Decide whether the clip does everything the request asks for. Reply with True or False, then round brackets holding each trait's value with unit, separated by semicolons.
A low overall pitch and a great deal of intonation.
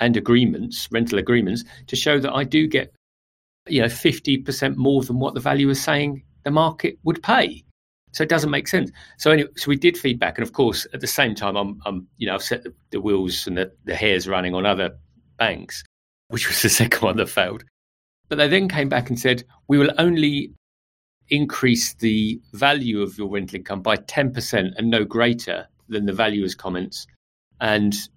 True (115 Hz; 6.6 semitones)